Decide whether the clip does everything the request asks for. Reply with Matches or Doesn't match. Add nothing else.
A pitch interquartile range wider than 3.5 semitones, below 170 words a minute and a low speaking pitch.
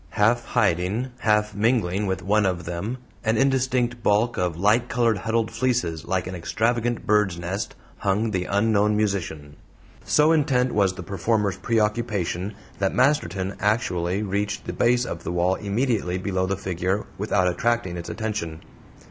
Matches